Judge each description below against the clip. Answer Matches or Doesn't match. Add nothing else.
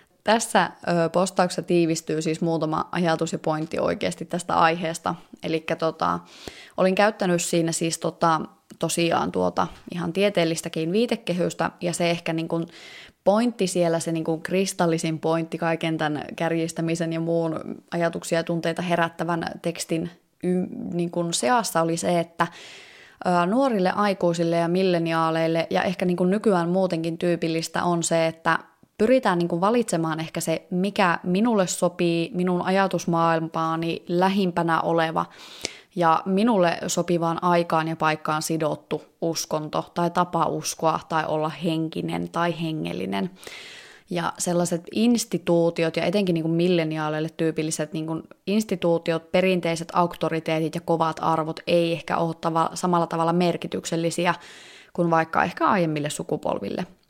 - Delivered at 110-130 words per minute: Matches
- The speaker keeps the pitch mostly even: Matches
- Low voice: Doesn't match